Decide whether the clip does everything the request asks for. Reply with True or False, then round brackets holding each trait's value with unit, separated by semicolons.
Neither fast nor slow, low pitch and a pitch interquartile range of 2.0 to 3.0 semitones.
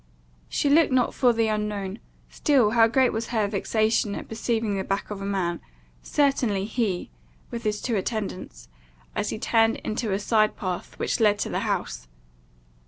False (170 wpm; 215 Hz; 2.7 semitones)